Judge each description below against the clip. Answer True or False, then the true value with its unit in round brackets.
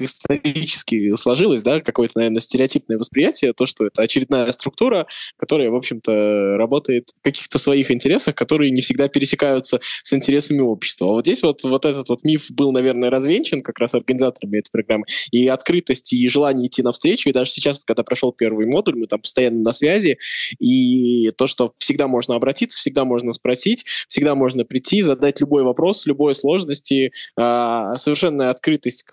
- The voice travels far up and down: False (2.8 semitones)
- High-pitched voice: False (130 Hz)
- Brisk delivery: True (165 wpm)